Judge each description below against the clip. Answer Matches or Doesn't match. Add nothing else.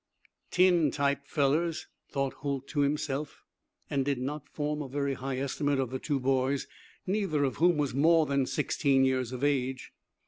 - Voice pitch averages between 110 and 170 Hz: Matches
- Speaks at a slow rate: Doesn't match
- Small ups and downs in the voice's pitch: Matches